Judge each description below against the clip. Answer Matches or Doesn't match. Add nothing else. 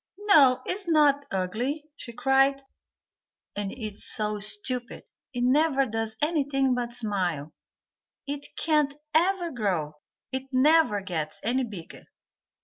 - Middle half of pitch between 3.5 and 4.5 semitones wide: Doesn't match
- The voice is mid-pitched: Doesn't match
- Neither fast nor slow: Doesn't match